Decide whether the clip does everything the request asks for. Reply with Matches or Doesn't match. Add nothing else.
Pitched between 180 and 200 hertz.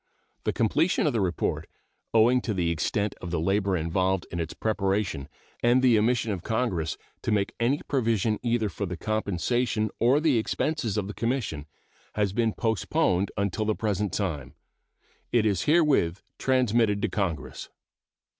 Doesn't match